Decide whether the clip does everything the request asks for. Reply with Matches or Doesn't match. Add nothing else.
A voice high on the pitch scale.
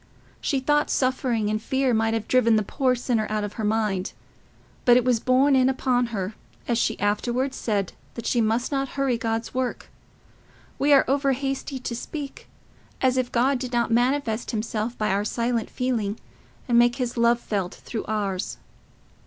Matches